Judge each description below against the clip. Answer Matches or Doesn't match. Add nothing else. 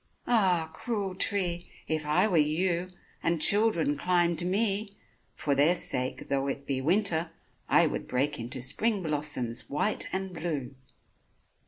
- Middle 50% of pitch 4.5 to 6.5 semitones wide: Matches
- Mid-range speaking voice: Matches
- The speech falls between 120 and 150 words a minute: Matches